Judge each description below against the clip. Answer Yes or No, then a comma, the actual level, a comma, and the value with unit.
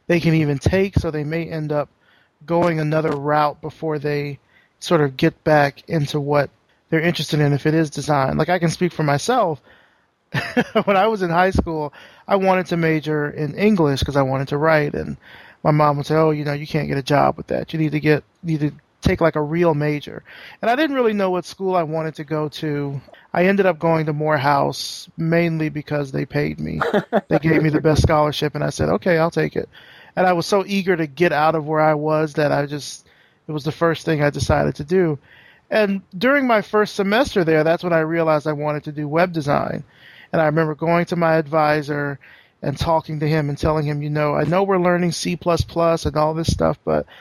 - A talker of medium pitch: Yes, medium, 155 Hz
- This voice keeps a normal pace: No, fast, 230 wpm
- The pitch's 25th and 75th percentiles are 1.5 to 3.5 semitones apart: Yes, narrow, 2.4 semitones